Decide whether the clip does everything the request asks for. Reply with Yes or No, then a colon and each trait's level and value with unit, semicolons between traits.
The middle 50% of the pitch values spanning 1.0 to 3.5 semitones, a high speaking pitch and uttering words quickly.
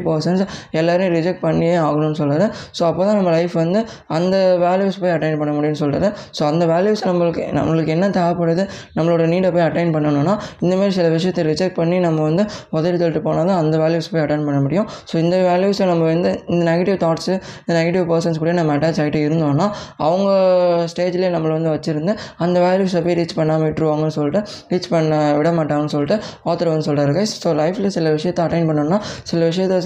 No: narrow, 2.6 semitones; medium, 170 Hz; fast, 180 wpm